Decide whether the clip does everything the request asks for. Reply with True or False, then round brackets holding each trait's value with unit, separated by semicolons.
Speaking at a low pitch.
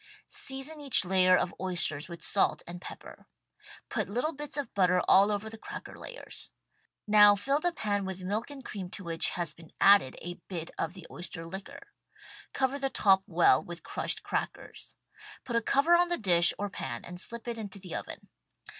False (200 Hz)